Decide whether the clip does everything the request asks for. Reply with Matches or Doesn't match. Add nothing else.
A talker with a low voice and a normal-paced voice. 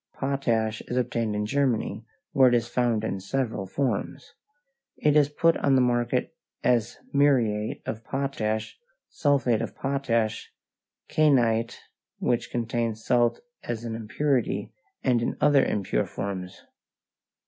Doesn't match